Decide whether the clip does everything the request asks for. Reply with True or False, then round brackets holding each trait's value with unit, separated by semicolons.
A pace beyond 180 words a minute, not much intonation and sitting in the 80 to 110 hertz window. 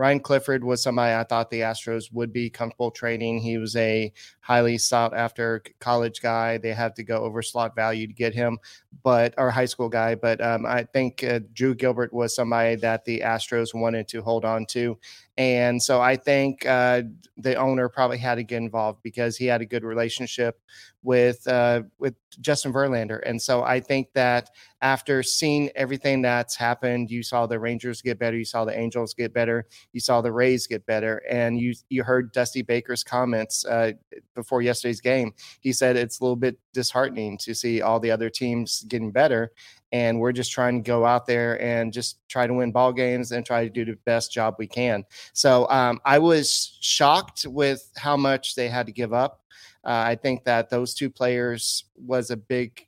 False (200 wpm; 1.5 semitones; 120 Hz)